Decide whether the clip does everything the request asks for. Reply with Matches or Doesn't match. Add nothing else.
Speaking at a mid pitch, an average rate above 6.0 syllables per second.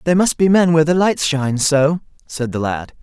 Doesn't match